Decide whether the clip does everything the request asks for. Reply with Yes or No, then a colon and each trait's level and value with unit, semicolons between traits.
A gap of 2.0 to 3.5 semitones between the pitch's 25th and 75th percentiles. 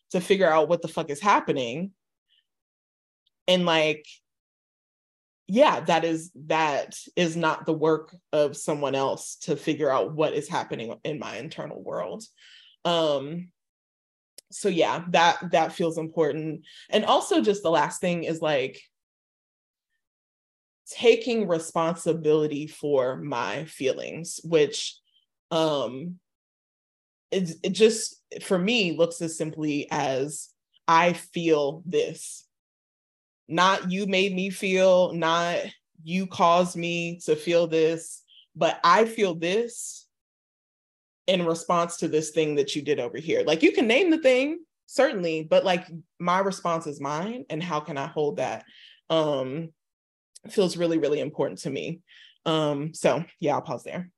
Yes: average, 3.2 semitones